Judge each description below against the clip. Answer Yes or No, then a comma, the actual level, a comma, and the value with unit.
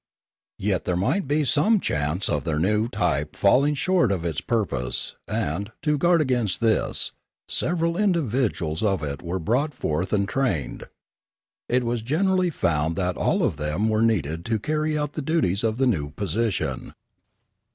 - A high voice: No, low, 110 Hz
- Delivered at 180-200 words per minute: No, average, 160 wpm